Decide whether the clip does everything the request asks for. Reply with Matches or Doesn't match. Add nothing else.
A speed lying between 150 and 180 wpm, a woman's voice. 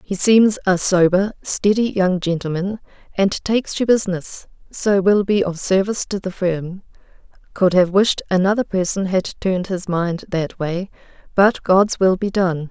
Matches